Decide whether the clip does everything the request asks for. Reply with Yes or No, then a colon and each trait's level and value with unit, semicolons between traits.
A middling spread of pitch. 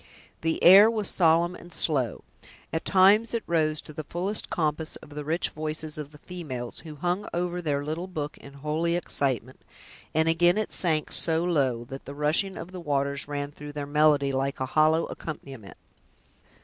Yes: average, 3.3 semitones